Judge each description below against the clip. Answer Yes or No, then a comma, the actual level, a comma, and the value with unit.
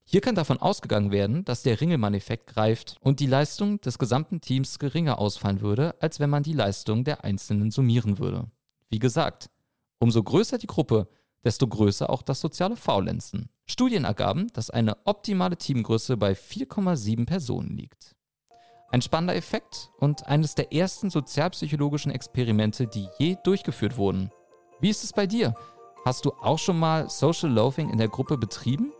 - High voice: No, low, 135 Hz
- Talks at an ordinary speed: Yes, average, 160 wpm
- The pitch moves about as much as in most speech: No, wide, 6.4 semitones